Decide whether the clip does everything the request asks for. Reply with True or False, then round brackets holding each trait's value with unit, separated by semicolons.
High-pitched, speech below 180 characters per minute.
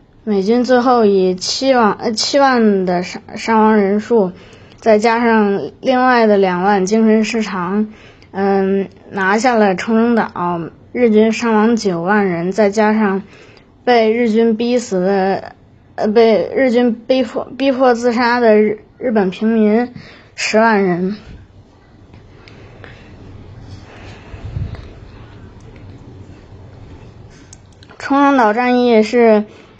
True (210 Hz; 150 characters per minute)